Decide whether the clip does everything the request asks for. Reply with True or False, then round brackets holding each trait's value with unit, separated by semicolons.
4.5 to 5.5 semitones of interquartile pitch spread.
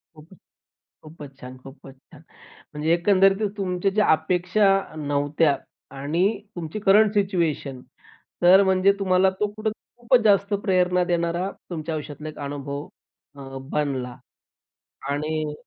True (5.0 semitones)